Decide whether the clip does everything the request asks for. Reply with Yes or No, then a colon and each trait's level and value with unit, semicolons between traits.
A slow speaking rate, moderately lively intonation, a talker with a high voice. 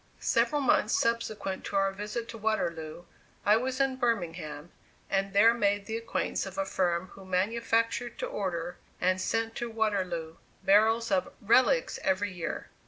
No: average, 155 wpm; average, 3.7 semitones; high, 205 Hz